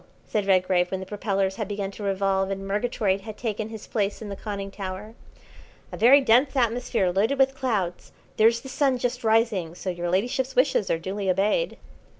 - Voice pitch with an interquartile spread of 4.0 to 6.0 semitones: No, average, 3.6 semitones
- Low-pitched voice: No, high, 205 Hz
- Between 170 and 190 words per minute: Yes, average, 185 wpm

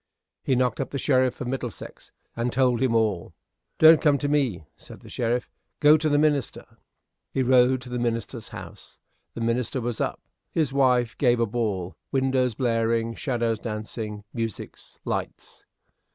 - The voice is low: Yes, low, 125 Hz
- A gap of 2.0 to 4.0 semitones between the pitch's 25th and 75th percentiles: Yes, narrow, 2.6 semitones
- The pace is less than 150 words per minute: No, average, 160 wpm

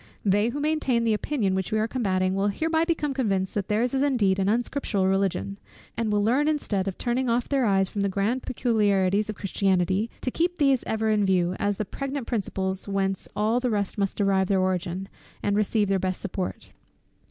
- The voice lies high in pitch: Yes, high, 205 Hz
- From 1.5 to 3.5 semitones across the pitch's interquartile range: No, average, 4.1 semitones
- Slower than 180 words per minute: No, average, 200 wpm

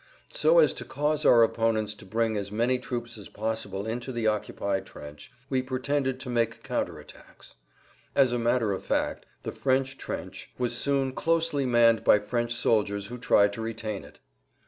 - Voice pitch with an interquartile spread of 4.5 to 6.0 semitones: No, average, 3.3 semitones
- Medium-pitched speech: No, low, 120 Hz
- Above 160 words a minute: Yes, average, 175 wpm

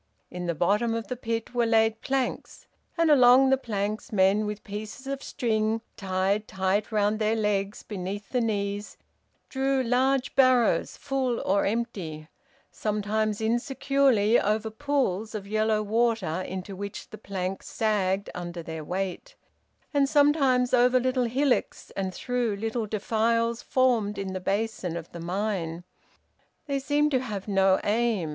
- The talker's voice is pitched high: Yes, high, 220 Hz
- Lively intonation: No, average, 4.0 semitones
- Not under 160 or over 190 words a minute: No, average, 145 wpm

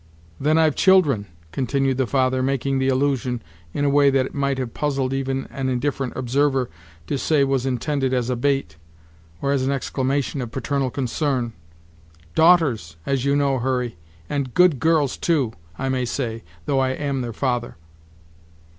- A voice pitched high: No, low, 135 Hz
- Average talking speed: Yes, average, 165 wpm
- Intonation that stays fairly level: Yes, narrow, 1.8 semitones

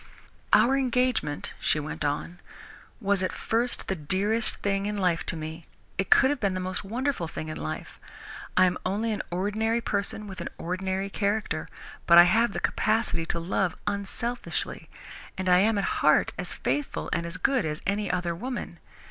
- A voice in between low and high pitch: No, high, 195 Hz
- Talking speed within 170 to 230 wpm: Yes, average, 180 wpm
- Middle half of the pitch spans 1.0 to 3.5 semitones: No, average, 4.0 semitones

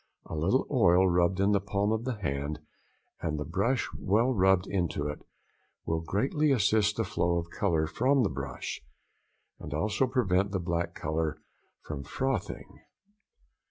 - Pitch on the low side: Yes, very low, 95 Hz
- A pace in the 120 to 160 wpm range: Yes, average, 155 wpm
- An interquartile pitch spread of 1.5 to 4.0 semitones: No, average, 5.0 semitones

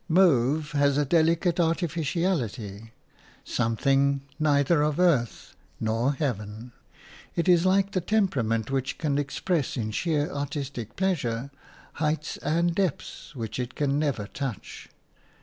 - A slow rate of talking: Yes, slow, 120 wpm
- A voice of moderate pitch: Yes, medium, 145 Hz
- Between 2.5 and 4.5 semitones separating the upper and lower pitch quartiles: No, average, 5.2 semitones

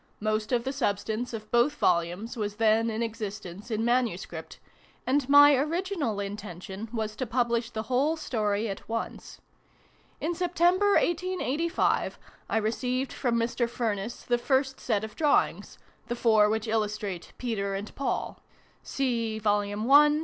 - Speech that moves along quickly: No, average, 140 wpm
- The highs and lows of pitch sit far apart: No, average, 3.9 semitones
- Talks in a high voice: Yes, high, 230 Hz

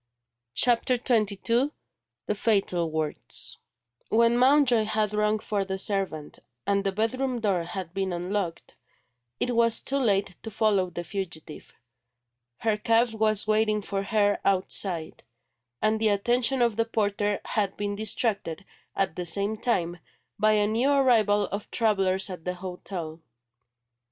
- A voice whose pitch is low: No, high, 205 Hz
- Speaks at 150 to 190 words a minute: No, average, 140 wpm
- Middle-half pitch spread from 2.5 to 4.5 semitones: Yes, average, 2.9 semitones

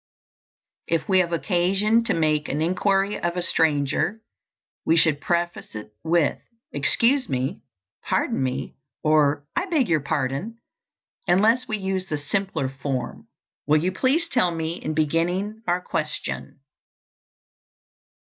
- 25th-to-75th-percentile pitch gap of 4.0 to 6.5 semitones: Yes, average, 4.6 semitones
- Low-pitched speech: No, medium, 170 Hz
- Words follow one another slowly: Yes, slow, 130 wpm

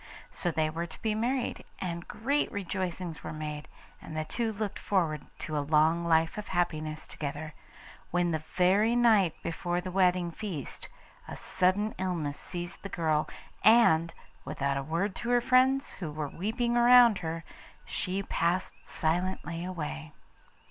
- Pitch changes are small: No, average, 4.5 semitones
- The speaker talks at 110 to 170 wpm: Yes, average, 155 wpm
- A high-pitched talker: No, medium, 175 Hz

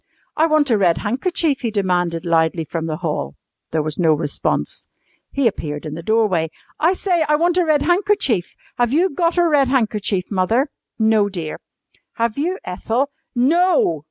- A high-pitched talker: Yes, high, 225 Hz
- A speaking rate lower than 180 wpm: Yes, average, 165 wpm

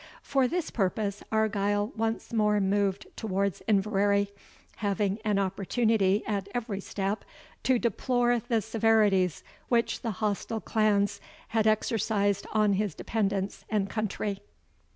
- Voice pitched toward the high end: Yes, high, 210 Hz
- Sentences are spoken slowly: Yes, slow, 120 wpm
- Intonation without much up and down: Yes, narrow, 2.0 semitones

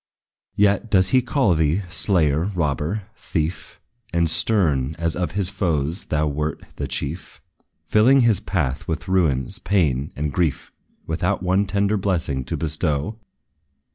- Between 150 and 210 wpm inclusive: No, average, 140 wpm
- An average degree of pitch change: Yes, average, 4.7 semitones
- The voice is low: Yes, very low, 85 Hz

